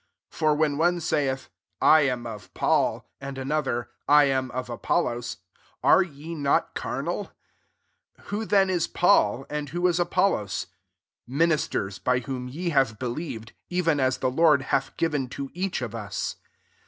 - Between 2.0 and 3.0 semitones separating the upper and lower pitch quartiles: No, average, 4.7 semitones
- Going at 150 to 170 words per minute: Yes, average, 160 wpm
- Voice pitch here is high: No, medium, 140 Hz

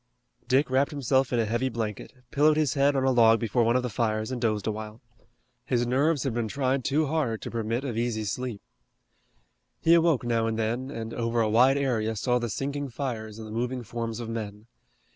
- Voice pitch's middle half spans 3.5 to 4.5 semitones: No, average, 3.0 semitones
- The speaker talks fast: Yes, fast, 215 wpm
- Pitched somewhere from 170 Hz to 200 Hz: No, low, 120 Hz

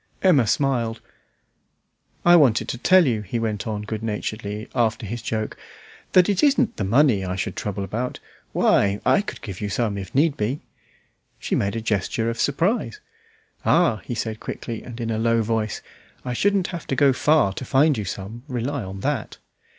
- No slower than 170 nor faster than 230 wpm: Yes, average, 185 wpm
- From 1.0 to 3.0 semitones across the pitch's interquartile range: No, average, 5.1 semitones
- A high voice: No, low, 115 Hz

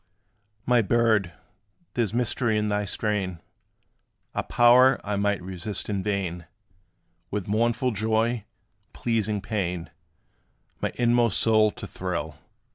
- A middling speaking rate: No, slow, 120 wpm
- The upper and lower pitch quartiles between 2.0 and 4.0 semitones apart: Yes, average, 3.2 semitones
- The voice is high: No, low, 105 Hz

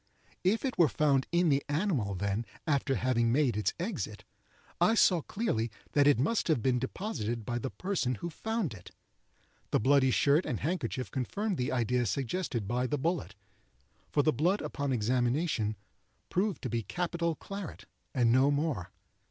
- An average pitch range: No, wide, 6.3 semitones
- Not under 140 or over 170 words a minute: Yes, average, 165 wpm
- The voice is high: No, medium, 140 Hz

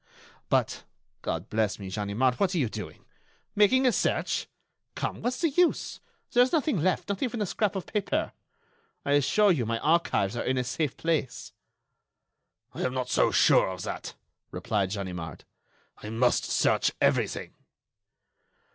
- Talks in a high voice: No, medium, 140 Hz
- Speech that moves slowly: No, average, 155 wpm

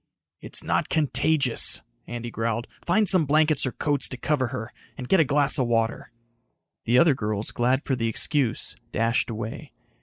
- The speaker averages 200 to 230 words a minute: No, average, 170 wpm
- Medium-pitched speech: No, low, 130 Hz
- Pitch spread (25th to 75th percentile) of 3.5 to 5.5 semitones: Yes, average, 4.3 semitones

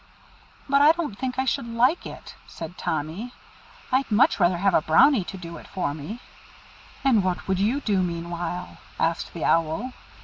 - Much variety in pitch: Yes, wide, 6.8 semitones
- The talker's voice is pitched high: Yes, high, 195 Hz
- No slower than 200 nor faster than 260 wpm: No, average, 180 wpm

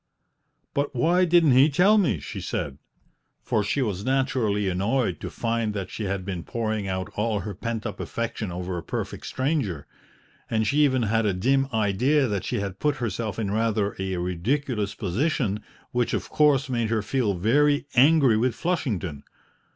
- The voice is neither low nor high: No, low, 115 Hz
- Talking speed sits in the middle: Yes, average, 175 wpm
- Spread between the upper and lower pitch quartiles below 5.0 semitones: No, average, 5.3 semitones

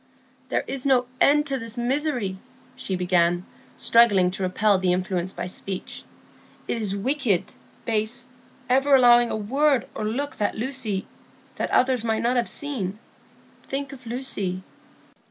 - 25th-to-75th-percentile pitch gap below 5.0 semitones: No, average, 5.3 semitones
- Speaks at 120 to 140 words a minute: Yes, slow, 135 wpm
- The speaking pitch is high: Yes, high, 235 Hz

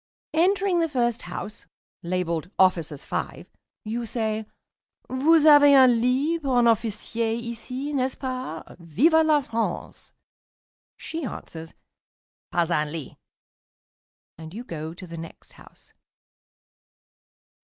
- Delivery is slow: Yes, slow, 120 wpm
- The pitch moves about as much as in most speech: No, wide, 7.8 semitones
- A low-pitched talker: No, high, 235 Hz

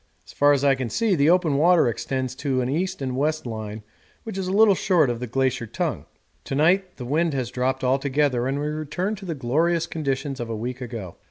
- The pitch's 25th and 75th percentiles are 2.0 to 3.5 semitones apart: No, average, 4.8 semitones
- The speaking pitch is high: No, medium, 140 Hz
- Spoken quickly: Yes, fast, 230 wpm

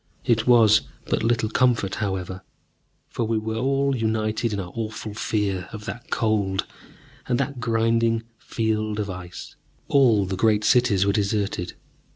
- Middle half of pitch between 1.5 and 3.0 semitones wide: Yes, narrow, 2.4 semitones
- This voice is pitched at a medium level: No, low, 110 Hz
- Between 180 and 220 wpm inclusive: No, average, 150 wpm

